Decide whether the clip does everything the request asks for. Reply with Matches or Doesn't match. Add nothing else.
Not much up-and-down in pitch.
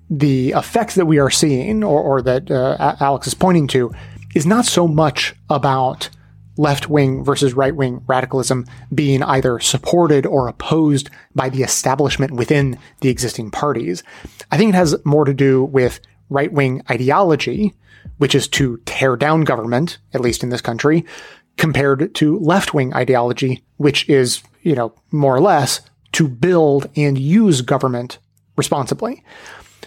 Doesn't match